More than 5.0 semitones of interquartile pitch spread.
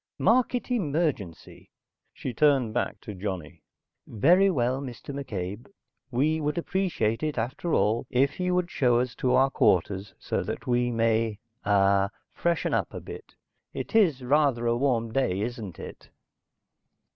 Yes: wide, 5.5 semitones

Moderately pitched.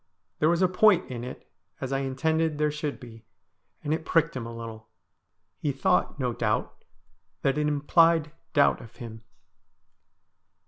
Yes: medium, 145 Hz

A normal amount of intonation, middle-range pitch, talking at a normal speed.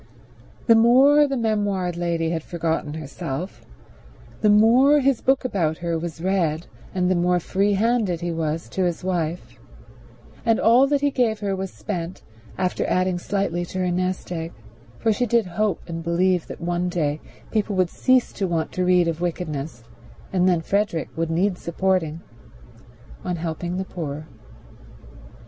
Yes: average, 3.7 semitones; medium, 180 Hz; average, 160 wpm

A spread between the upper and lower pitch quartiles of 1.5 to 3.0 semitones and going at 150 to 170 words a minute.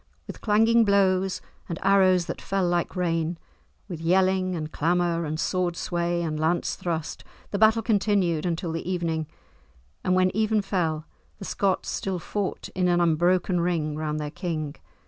Yes: narrow, 2.5 semitones; average, 160 wpm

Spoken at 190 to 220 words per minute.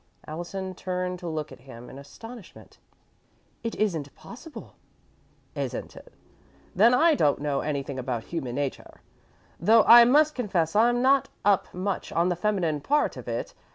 No: average, 155 wpm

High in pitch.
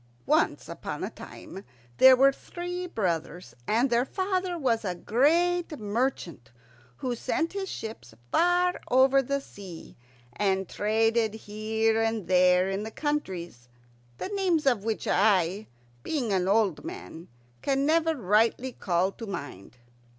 Yes: high, 225 Hz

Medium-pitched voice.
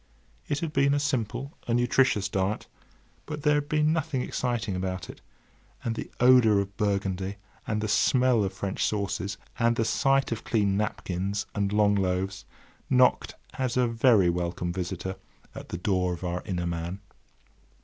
No: low, 105 Hz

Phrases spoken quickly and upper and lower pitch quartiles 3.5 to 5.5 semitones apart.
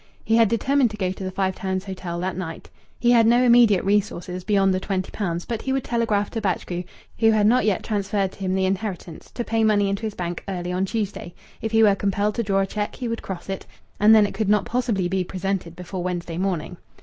No: fast, 240 wpm; average, 2.9 semitones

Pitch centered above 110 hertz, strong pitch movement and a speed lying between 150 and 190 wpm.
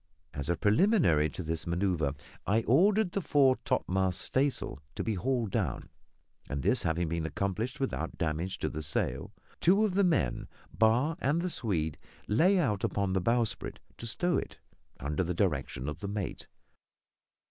No: low, 100 Hz; wide, 8.8 semitones; average, 165 wpm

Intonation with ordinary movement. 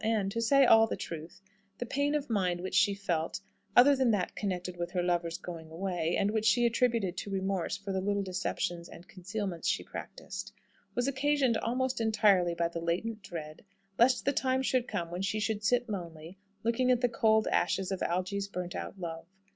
Yes: average, 4.8 semitones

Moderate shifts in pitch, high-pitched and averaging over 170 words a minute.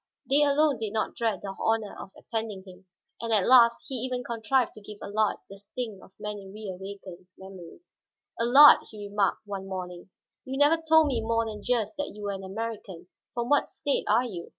Yes: average, 4.0 semitones; high, 220 Hz; average, 195 wpm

